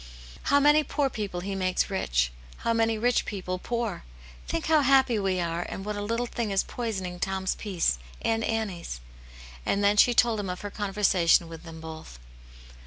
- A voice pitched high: Yes, high, 200 Hz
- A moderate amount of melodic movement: Yes, average, 4.1 semitones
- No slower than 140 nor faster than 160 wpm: No, average, 180 wpm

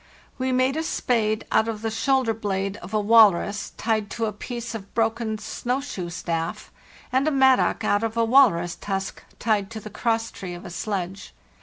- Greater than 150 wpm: Yes, average, 190 wpm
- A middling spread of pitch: Yes, average, 3.1 semitones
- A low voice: No, high, 220 Hz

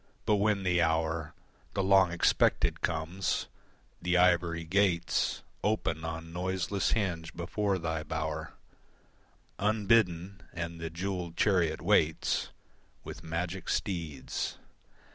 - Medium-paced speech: No, slow, 105 wpm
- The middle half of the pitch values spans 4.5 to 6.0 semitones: No, average, 2.8 semitones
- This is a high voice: No, very low, 85 Hz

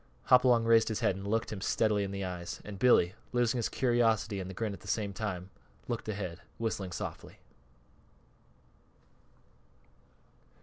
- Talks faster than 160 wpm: No, average, 150 wpm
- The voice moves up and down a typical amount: Yes, average, 3.1 semitones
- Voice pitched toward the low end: Yes, low, 105 Hz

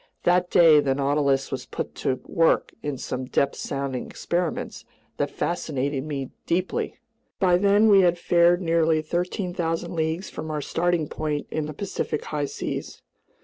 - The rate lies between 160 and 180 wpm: No, average, 150 wpm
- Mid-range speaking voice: Yes, medium, 160 Hz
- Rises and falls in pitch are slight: No, average, 3.6 semitones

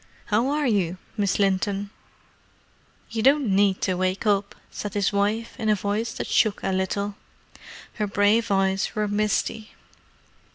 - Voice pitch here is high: Yes, high, 205 Hz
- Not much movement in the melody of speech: Yes, narrow, 1.8 semitones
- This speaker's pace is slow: No, average, 150 wpm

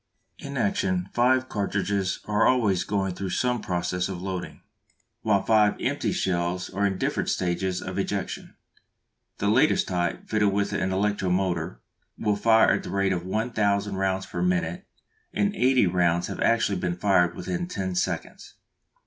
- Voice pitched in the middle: No, low, 100 Hz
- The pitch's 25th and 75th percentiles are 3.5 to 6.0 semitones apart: No, average, 2.9 semitones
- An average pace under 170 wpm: Yes, average, 160 wpm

